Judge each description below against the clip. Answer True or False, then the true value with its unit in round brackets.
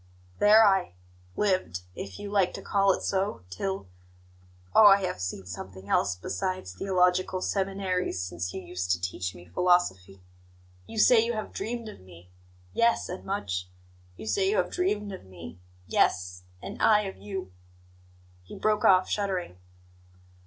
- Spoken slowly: False (160 wpm)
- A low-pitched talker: False (180 Hz)